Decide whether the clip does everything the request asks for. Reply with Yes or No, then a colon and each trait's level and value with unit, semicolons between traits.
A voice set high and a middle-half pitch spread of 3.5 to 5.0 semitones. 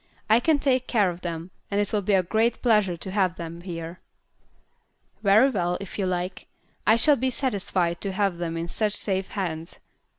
Yes: high, 195 Hz; average, 3.9 semitones